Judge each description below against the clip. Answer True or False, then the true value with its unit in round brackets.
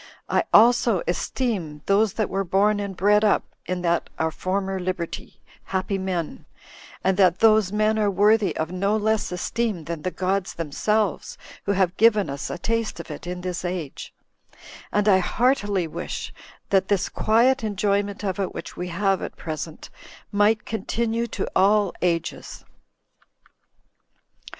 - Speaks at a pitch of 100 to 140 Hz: False (195 Hz)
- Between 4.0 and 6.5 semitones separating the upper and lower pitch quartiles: False (2.9 semitones)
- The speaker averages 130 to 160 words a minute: True (150 wpm)